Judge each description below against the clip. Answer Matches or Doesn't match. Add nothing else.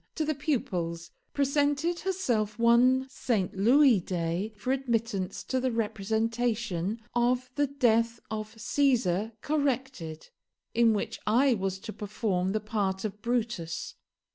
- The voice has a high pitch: Matches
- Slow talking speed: Matches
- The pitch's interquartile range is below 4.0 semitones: Doesn't match